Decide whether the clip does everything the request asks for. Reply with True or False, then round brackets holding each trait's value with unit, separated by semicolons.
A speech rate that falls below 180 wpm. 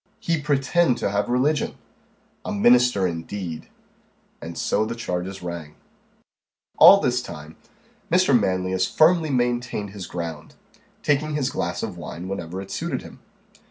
True (135 wpm)